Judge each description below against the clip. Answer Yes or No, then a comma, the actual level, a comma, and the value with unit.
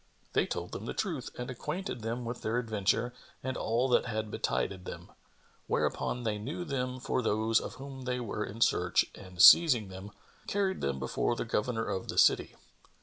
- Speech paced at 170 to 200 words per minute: Yes, average, 185 wpm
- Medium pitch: No, low, 115 Hz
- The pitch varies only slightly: No, average, 3.2 semitones